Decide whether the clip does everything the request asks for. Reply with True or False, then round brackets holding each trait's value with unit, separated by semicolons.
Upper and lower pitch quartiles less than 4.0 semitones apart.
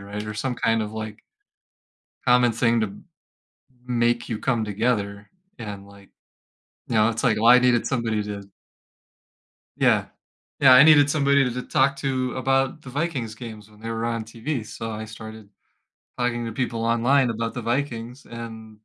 True (2.5 semitones)